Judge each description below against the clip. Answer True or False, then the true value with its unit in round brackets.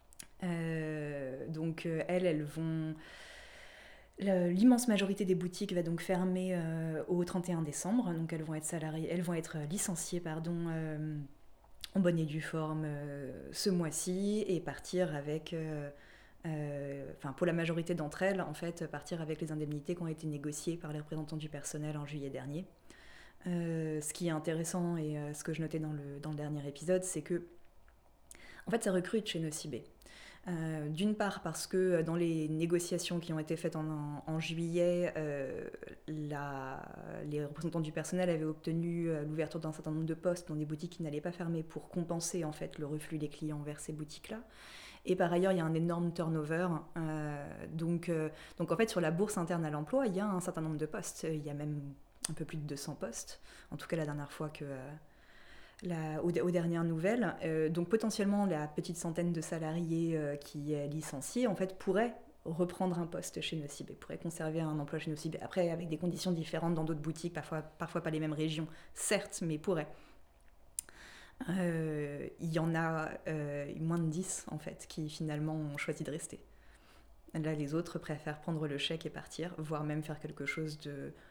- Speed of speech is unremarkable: True (195 wpm)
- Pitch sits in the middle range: True (160 Hz)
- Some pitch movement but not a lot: False (2.3 semitones)